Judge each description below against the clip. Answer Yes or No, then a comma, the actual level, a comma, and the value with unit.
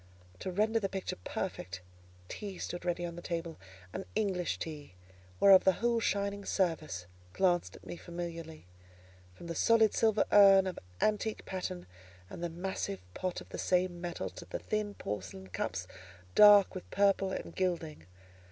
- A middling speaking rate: Yes, average, 155 wpm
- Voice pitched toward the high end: No, medium, 180 Hz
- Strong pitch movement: No, average, 3.3 semitones